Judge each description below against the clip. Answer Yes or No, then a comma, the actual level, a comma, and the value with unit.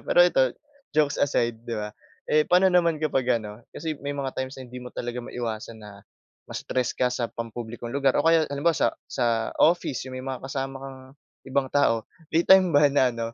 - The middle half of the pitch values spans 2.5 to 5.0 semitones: Yes, average, 3.4 semitones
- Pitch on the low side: Yes, low, 130 Hz